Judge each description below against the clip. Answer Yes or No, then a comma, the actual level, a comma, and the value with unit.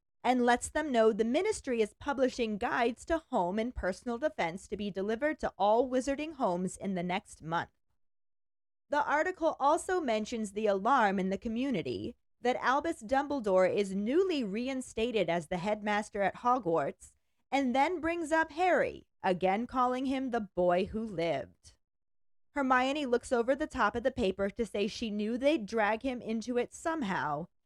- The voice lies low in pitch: No, high, 235 Hz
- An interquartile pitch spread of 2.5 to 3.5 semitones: No, average, 5.2 semitones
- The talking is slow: No, average, 165 wpm